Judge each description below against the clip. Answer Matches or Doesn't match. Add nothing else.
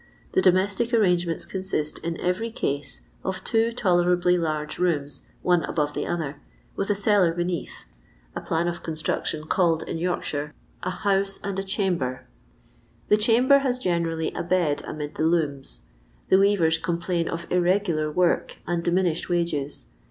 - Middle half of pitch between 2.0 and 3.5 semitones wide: Matches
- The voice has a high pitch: Doesn't match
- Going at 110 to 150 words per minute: Doesn't match